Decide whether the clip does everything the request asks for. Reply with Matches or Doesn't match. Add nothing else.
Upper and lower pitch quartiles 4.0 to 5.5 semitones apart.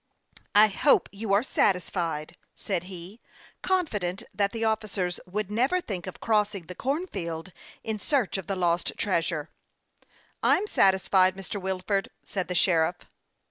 Doesn't match